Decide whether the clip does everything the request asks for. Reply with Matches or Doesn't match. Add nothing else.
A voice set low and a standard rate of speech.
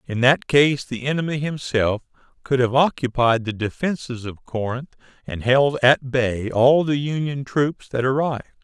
Matches